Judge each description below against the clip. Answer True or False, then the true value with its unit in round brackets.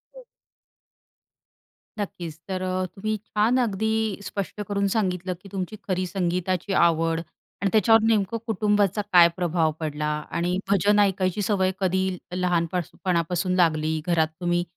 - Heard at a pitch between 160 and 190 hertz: True (185 Hz)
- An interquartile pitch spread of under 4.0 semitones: True (2.8 semitones)